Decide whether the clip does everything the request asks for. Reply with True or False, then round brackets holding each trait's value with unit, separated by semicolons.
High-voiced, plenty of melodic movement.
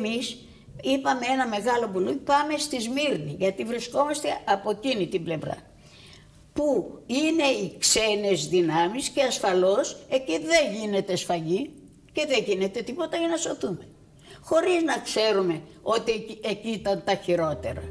True (220 Hz; 6.5 semitones)